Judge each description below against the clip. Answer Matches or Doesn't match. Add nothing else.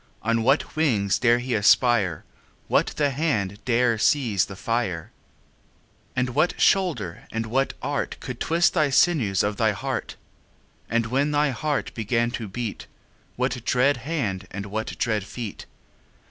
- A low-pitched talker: Matches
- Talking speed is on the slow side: Doesn't match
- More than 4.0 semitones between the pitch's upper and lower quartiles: Matches